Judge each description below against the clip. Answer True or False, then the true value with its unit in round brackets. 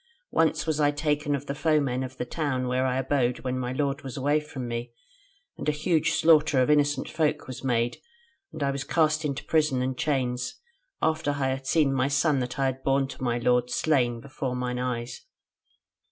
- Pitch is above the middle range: False (135 Hz)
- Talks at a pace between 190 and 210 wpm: True (200 wpm)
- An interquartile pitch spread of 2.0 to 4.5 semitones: True (2.9 semitones)